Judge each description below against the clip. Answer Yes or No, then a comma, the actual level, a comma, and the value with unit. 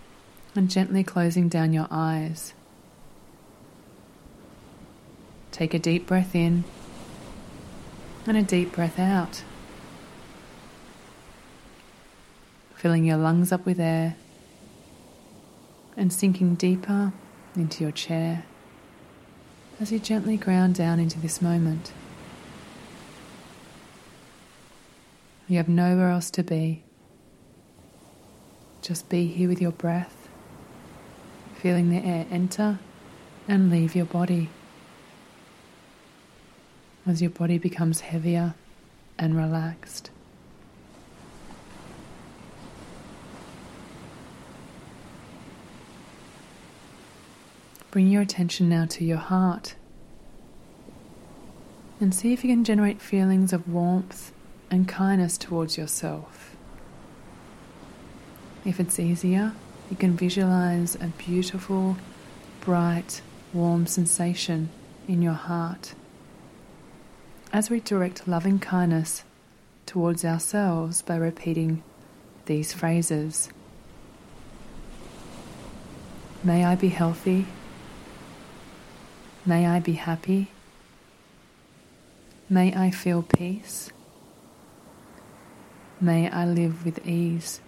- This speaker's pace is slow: Yes, slow, 85 wpm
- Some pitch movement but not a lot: No, narrow, 2.0 semitones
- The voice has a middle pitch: Yes, medium, 175 Hz